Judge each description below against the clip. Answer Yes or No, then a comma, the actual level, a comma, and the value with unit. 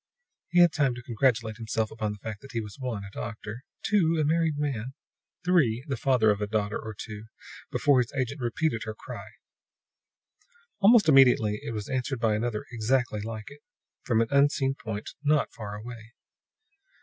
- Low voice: Yes, low, 120 Hz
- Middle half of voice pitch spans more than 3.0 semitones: Yes, average, 4.3 semitones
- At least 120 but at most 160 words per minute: No, average, 175 wpm